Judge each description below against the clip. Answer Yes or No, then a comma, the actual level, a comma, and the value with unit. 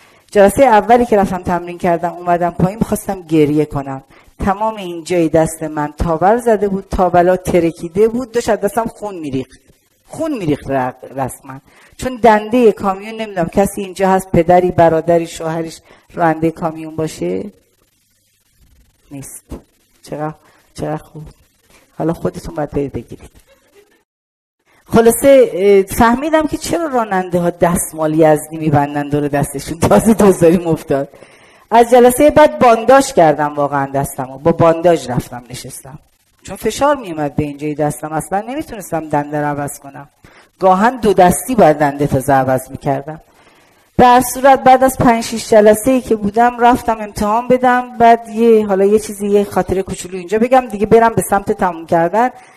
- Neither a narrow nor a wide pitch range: No, wide, 7.0 semitones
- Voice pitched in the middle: Yes, medium, 180 Hz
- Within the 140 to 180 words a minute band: Yes, average, 145 wpm